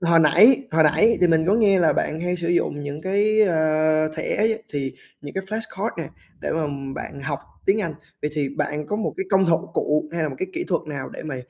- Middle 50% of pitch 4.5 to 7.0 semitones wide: No, average, 4.0 semitones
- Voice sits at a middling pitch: Yes, medium, 165 Hz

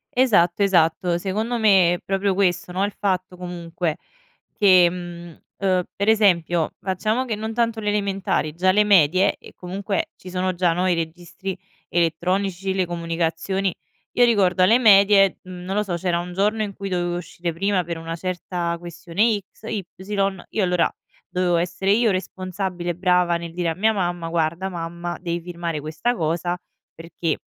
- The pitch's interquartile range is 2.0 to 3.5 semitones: Yes, narrow, 2.4 semitones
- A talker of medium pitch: Yes, medium, 180 Hz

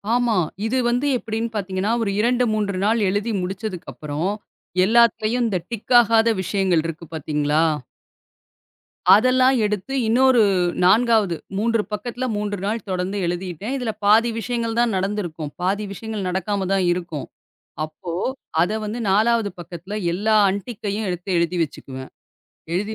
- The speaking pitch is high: Yes, high, 205 Hz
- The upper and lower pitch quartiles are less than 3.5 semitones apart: No, average, 4.0 semitones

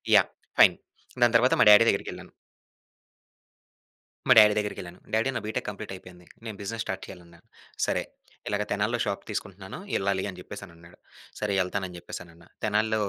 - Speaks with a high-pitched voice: No, low, 100 Hz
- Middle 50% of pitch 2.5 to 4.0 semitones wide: Yes, average, 2.9 semitones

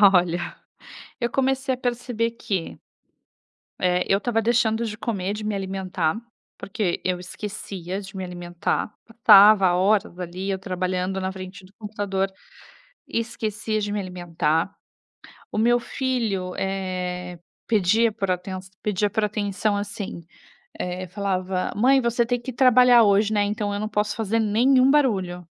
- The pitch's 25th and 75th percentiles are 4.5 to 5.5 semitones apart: No, average, 3.4 semitones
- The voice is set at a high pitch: Yes, high, 205 Hz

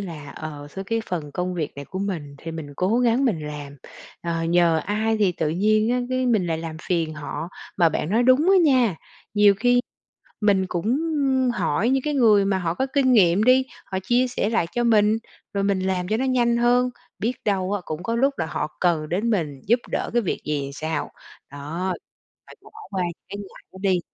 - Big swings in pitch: Yes, wide, 6.3 semitones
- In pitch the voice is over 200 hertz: No, high, 195 Hz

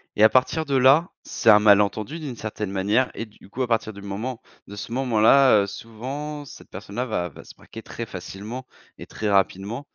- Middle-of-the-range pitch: No, low, 110 Hz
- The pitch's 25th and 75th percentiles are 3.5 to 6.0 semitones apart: Yes, average, 4.2 semitones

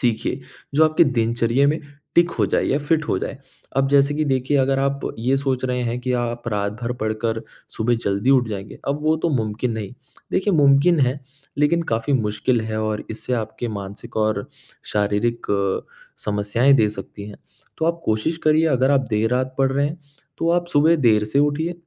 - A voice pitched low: Yes, low, 125 Hz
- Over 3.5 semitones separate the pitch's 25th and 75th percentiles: Yes, average, 4.5 semitones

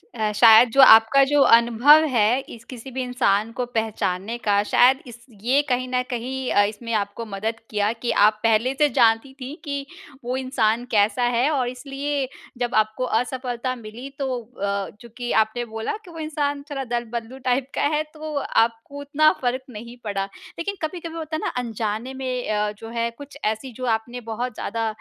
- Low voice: No, high, 245 Hz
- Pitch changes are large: No, average, 3.3 semitones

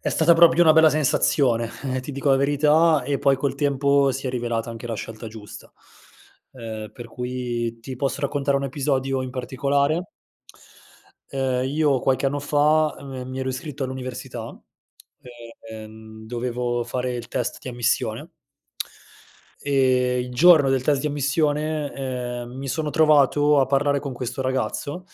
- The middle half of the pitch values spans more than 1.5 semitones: Yes, narrow, 2.6 semitones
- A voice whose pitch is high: No, low, 135 Hz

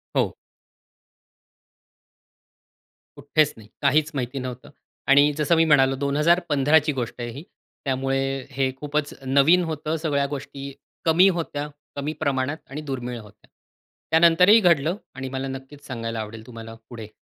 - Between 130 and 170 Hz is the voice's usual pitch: Yes, medium, 140 Hz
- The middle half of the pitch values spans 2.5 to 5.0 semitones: Yes, average, 2.9 semitones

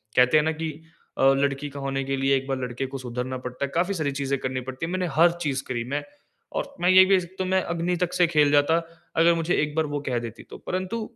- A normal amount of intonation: Yes, average, 4.3 semitones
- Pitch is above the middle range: No, medium, 145 Hz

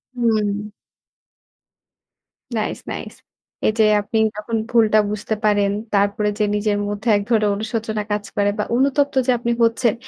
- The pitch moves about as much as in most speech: No, narrow, 1.8 semitones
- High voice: Yes, high, 215 Hz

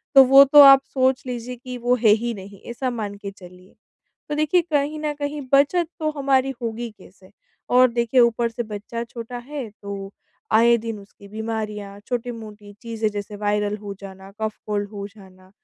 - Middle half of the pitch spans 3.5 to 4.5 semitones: Yes, average, 3.9 semitones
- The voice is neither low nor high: No, high, 230 Hz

